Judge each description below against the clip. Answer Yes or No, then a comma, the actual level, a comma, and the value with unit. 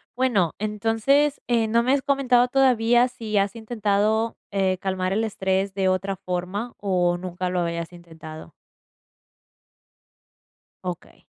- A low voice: No, high, 200 Hz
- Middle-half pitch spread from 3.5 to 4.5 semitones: Yes, average, 4.2 semitones